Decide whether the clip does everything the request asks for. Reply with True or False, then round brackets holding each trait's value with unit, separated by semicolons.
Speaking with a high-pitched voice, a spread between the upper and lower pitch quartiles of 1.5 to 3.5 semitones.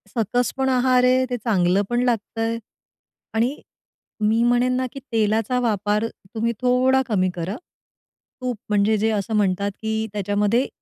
True (225 Hz; 3.2 semitones)